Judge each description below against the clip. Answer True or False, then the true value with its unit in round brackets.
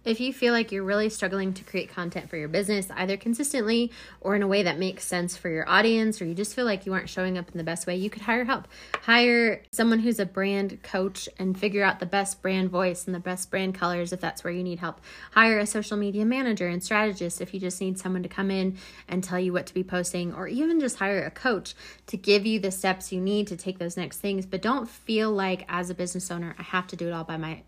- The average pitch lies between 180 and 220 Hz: True (190 Hz)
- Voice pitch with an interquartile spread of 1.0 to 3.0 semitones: True (2.7 semitones)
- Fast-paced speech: True (265 wpm)